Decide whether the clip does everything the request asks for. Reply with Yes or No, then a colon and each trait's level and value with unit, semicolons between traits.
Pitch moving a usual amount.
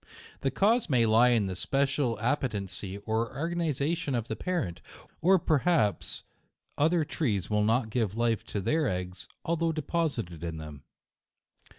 No: wide, 7.4 semitones